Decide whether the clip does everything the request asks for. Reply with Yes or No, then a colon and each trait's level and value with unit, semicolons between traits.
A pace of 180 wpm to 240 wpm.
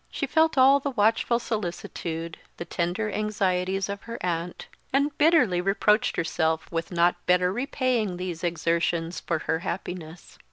No: average, 145 wpm